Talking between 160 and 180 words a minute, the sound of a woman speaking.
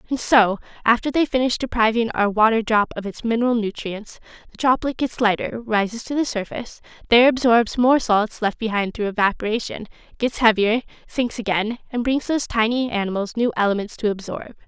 Yes: average, 170 wpm; female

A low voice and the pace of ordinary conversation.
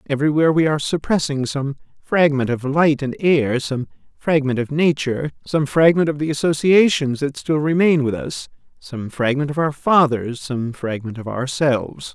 No: medium, 145 Hz; average, 165 wpm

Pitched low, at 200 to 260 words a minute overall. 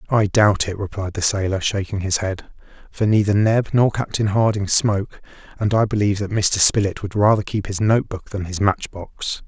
Yes: low, 100 Hz; fast, 205 wpm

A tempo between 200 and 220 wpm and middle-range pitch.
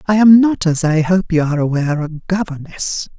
Yes: fast, 205 wpm; medium, 170 Hz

